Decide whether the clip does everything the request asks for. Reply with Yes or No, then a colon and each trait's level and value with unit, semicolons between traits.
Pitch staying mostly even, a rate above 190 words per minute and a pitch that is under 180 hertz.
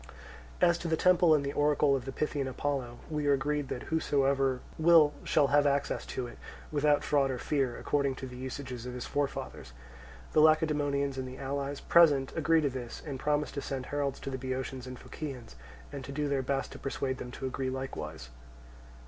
Yes: narrow, 2.1 semitones; average, 200 wpm; medium, 140 Hz